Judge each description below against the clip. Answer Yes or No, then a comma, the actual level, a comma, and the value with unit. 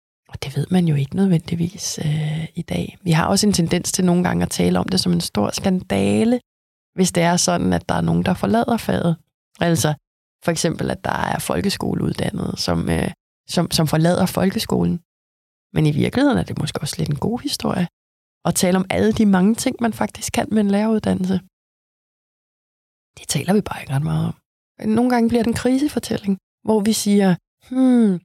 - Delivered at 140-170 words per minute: No, average, 195 wpm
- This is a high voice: No, medium, 175 Hz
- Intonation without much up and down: No, wide, 5.6 semitones